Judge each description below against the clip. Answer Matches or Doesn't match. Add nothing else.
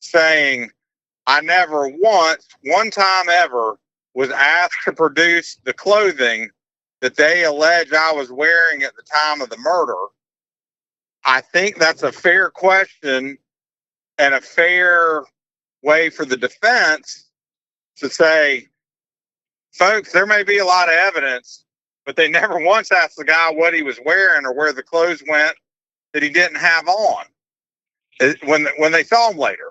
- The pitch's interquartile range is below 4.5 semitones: Matches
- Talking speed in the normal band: Matches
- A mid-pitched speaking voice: Matches